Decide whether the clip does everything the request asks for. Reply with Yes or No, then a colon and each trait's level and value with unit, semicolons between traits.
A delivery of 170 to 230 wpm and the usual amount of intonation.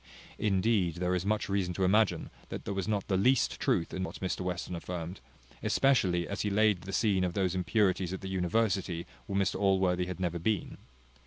No: average, 195 wpm; narrow, 1.9 semitones